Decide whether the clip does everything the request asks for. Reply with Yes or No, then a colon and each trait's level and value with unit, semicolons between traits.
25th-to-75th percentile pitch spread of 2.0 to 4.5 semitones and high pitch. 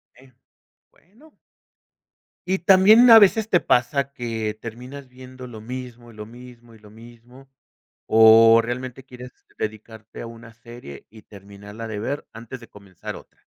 No: average, 2.8 semitones; low, 120 Hz